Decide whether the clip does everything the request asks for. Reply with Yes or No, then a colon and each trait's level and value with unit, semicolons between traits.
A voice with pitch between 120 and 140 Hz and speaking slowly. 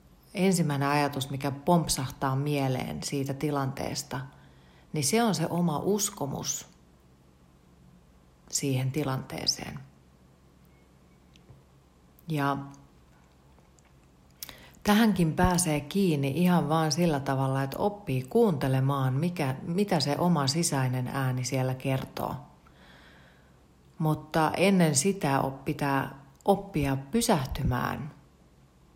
Yes: low, 135 Hz; slow, 85 wpm